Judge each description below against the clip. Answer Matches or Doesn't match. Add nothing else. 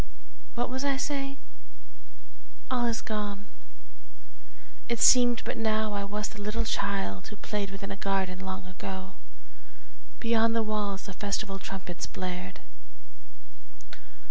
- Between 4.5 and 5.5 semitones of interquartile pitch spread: Doesn't match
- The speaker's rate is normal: Doesn't match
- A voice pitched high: Matches